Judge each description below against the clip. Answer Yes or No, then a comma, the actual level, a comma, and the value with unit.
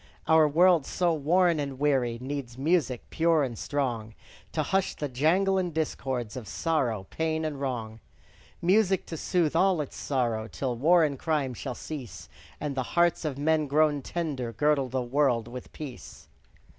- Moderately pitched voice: Yes, medium, 145 Hz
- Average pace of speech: Yes, average, 165 wpm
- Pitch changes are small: No, average, 4.1 semitones